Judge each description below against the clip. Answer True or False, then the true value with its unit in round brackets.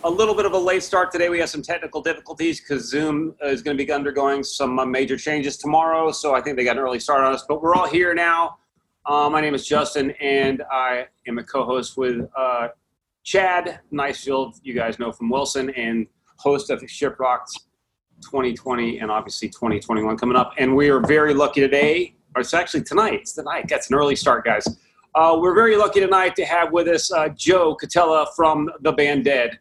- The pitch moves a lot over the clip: False (3.7 semitones)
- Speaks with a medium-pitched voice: True (145 Hz)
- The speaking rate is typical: False (210 wpm)